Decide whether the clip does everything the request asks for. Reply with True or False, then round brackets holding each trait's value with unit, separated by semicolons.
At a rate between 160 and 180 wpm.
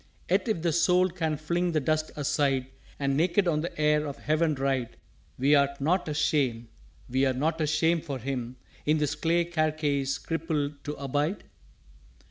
True (165 wpm)